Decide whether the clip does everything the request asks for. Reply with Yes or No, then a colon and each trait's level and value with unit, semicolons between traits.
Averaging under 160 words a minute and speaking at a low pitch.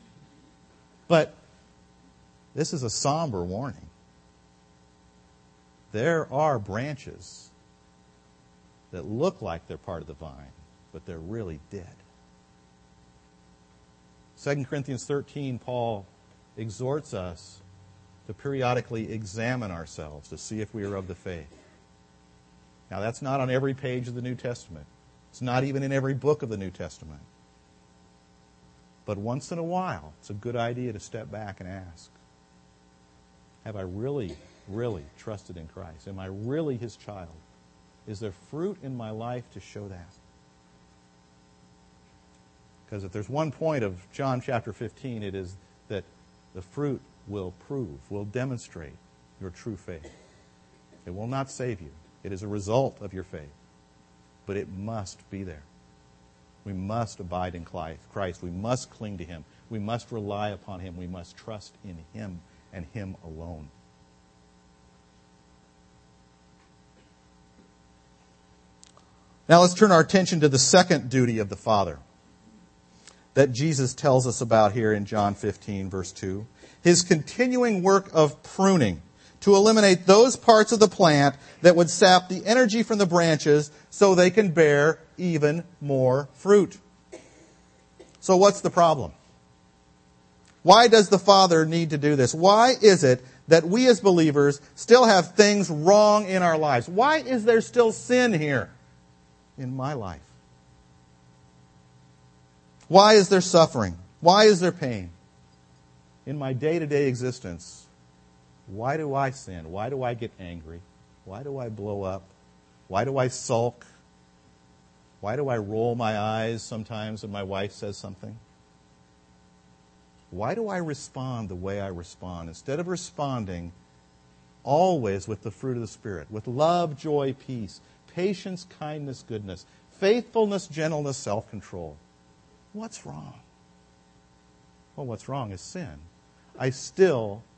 Yes: average, 140 wpm; low, 100 Hz